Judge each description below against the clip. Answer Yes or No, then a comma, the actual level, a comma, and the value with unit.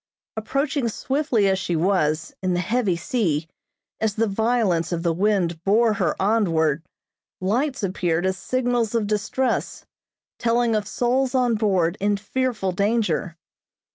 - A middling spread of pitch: Yes, average, 5.0 semitones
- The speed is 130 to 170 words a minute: Yes, average, 140 wpm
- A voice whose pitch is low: No, high, 205 Hz